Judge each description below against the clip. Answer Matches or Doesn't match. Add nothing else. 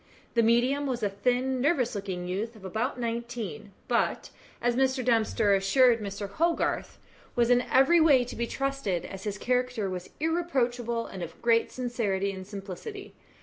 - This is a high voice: Matches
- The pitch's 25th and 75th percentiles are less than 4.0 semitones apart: Doesn't match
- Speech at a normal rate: Matches